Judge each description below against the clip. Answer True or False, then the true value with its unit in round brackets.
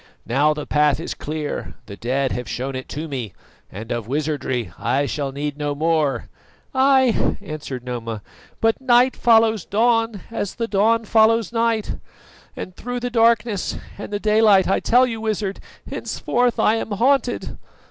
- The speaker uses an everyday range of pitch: False (8.6 semitones)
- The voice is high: True (195 Hz)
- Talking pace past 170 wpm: False (155 wpm)